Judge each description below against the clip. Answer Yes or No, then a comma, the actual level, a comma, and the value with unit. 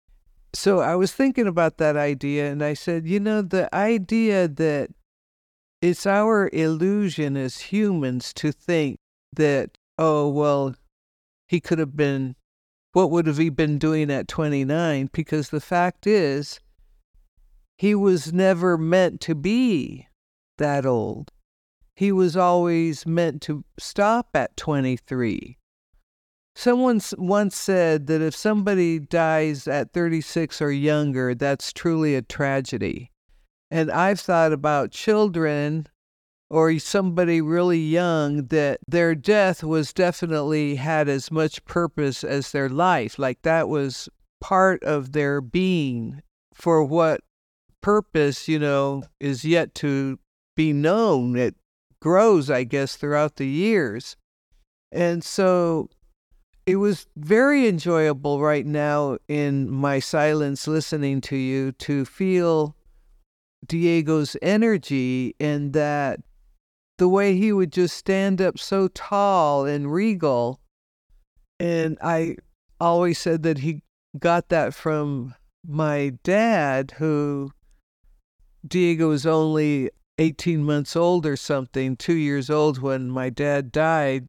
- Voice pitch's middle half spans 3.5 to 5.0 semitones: Yes, average, 3.9 semitones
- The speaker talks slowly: Yes, slow, 125 wpm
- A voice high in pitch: No, medium, 155 Hz